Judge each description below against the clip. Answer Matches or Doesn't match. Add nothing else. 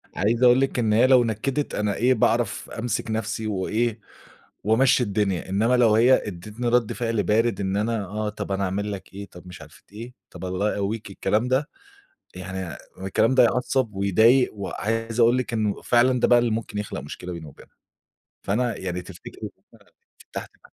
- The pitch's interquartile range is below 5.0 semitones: Matches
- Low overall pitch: Matches